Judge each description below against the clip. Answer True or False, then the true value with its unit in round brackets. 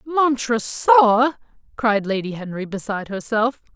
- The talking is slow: True (95 wpm)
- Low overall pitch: False (225 Hz)